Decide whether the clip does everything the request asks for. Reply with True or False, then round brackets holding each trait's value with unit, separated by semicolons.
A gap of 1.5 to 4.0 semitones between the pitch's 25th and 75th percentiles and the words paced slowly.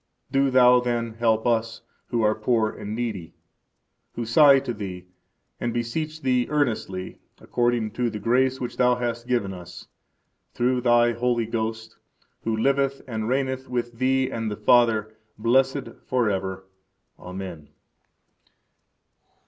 True (2.5 semitones; 130 wpm)